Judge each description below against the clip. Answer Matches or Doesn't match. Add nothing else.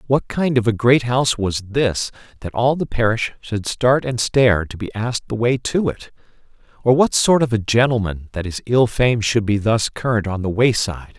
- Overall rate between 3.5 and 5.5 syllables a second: Matches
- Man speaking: Matches